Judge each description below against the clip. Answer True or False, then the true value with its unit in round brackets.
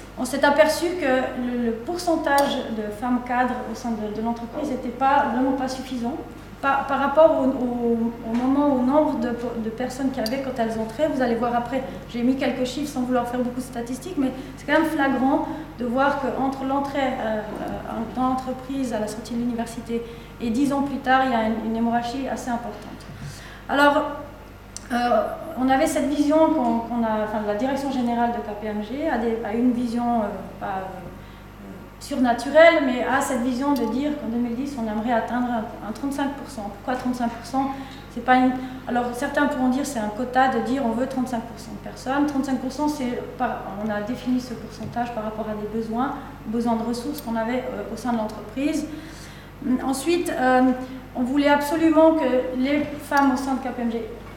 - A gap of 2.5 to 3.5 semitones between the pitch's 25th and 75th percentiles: True (2.9 semitones)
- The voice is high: True (255 Hz)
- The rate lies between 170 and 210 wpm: True (190 wpm)